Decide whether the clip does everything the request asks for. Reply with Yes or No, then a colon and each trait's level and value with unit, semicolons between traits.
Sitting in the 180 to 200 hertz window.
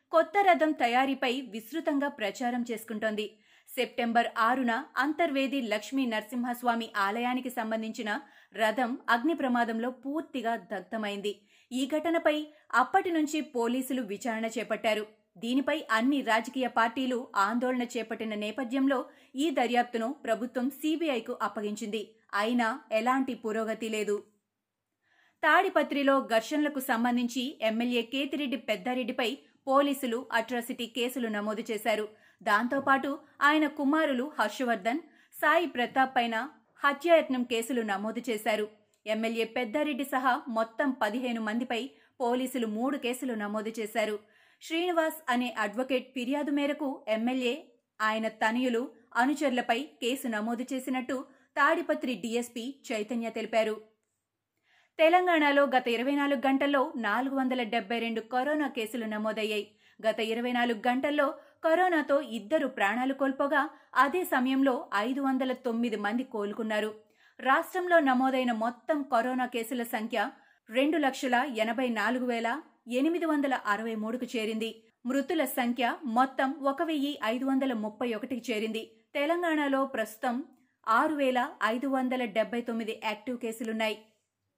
No: high, 245 Hz